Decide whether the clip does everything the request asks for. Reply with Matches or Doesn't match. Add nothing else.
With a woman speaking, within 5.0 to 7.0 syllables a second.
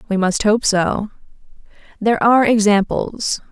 Doesn't match